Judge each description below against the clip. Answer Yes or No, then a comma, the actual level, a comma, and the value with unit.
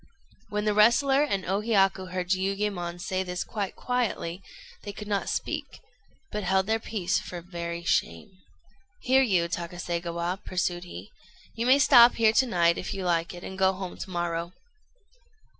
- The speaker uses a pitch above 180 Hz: Yes, high, 190 Hz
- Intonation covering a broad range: No, average, 3.4 semitones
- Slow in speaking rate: No, average, 165 wpm